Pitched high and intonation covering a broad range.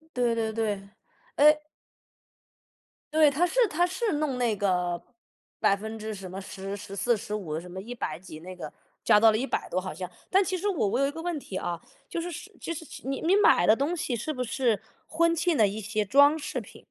Yes: high, 230 Hz; wide, 7.9 semitones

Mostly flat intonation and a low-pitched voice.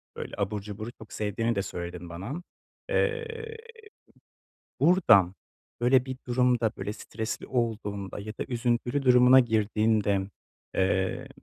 No: average, 3.7 semitones; low, 110 Hz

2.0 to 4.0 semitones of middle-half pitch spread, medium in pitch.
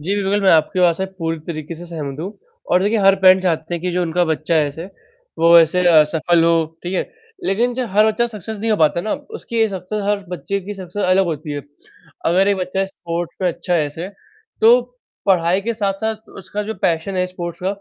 Yes: average, 3.1 semitones; medium, 180 Hz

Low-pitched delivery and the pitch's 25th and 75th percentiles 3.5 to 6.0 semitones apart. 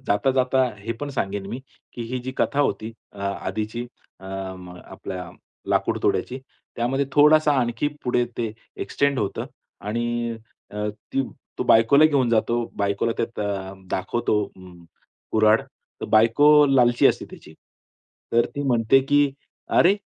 Yes: low, 115 Hz; average, 4.4 semitones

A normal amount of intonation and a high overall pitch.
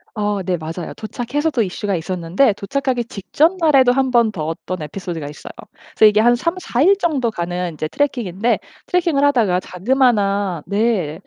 No: wide, 6.6 semitones; high, 215 Hz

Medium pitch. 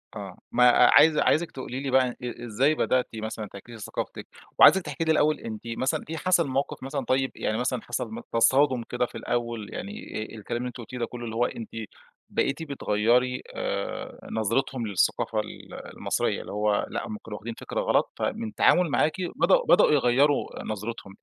No: low, 125 Hz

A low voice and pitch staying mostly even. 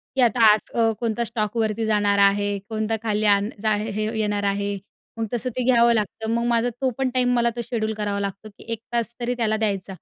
No: high, 220 Hz; narrow, 2.3 semitones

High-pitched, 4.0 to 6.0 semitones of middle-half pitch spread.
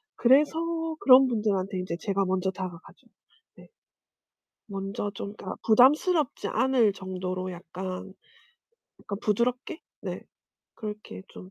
Yes: high, 205 Hz; average, 5.3 semitones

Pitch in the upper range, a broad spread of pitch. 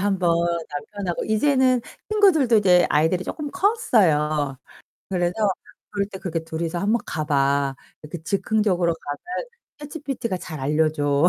No: medium, 180 Hz; wide, 6.4 semitones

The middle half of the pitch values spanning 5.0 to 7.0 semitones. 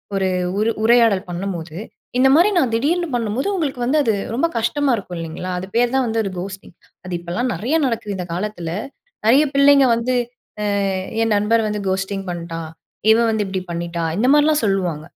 Yes: wide, 5.4 semitones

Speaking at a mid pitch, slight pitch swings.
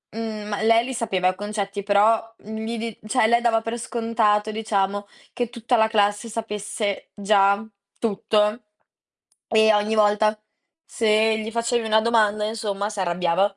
No: high, 215 Hz; narrow, 1.7 semitones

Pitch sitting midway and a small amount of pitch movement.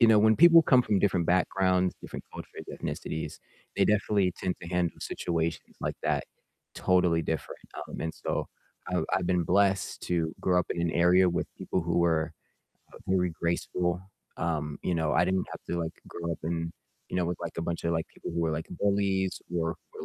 No: very low, 90 Hz; narrow, 2.1 semitones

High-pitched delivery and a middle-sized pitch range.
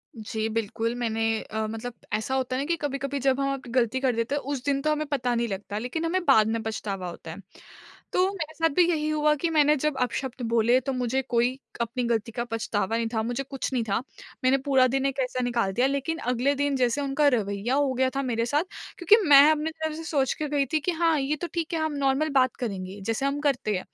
Yes: very high, 260 Hz; average, 3.9 semitones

